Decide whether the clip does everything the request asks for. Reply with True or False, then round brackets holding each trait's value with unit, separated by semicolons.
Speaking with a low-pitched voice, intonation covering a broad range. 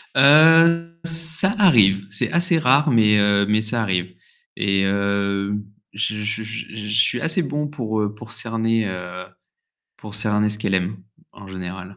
True (110 Hz; 6.3 semitones)